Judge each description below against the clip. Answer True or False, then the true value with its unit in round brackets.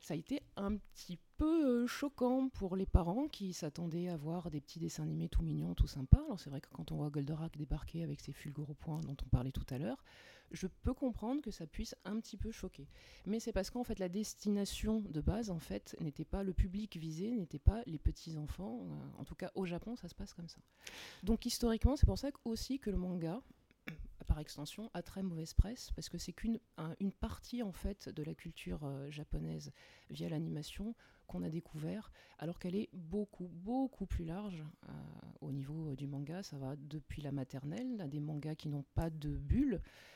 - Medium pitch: True (175 Hz)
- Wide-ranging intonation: True (6.0 semitones)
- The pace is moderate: True (210 wpm)